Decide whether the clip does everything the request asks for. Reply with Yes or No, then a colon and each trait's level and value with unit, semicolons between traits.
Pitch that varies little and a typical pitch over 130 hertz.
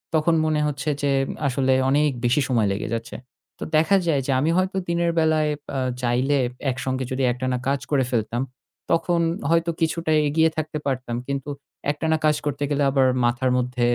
No: average, 3.5 semitones; medium, 140 Hz